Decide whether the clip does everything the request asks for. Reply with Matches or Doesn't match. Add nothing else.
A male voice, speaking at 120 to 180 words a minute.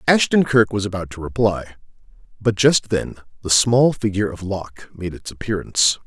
Matches